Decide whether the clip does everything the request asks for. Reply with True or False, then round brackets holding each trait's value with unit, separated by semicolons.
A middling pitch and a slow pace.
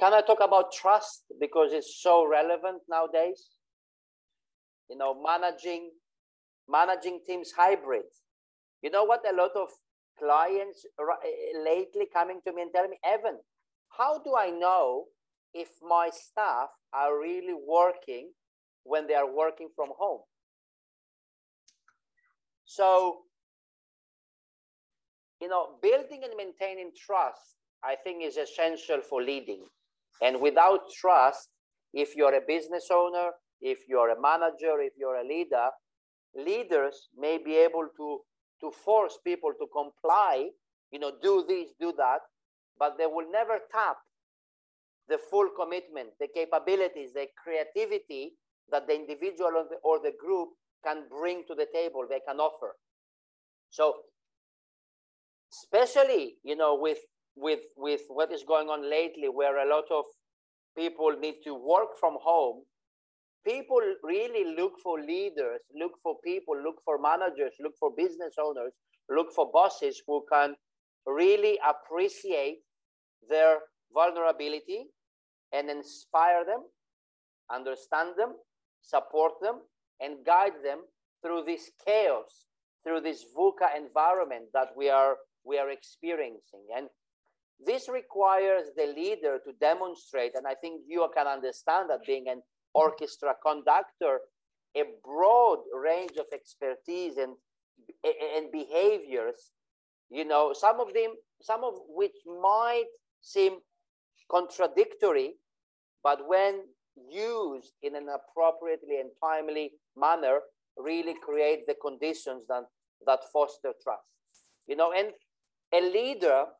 True (175 Hz; 130 wpm)